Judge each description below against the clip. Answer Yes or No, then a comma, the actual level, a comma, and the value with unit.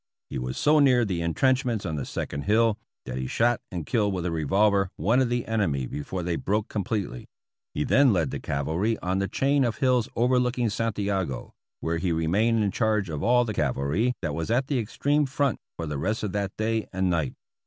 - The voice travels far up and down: Yes, wide, 6.3 semitones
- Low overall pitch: Yes, low, 105 Hz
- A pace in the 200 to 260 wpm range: Yes, fast, 205 wpm